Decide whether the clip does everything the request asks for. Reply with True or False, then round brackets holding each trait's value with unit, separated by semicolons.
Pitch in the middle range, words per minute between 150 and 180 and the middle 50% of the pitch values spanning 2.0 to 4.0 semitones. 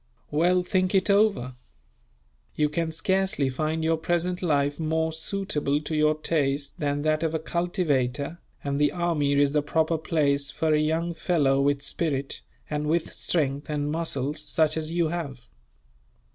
True (155 Hz; 160 wpm; 2.7 semitones)